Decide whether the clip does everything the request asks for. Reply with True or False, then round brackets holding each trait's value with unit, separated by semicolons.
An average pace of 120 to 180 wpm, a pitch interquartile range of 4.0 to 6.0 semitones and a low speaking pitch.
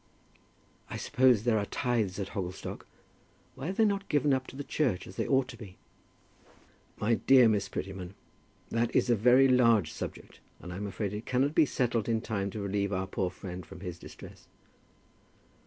False (190 wpm; 4.7 semitones; 110 Hz)